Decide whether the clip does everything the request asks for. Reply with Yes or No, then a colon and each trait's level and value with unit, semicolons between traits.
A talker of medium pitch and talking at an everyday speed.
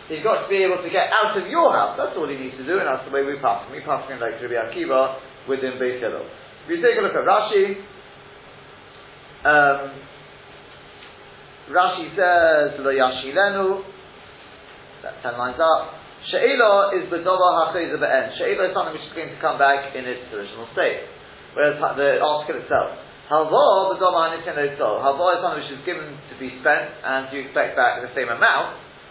Yes: medium, 155 Hz; average, 180 wpm